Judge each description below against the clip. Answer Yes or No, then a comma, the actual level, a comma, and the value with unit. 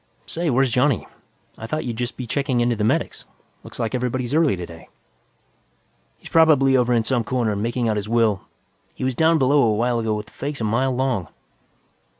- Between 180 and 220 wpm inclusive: Yes, average, 200 wpm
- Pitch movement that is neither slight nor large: Yes, average, 3.1 semitones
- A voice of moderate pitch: No, low, 120 Hz